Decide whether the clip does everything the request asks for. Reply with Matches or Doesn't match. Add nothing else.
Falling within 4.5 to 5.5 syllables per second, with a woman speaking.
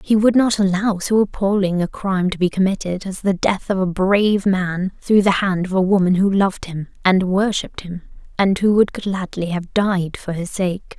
Matches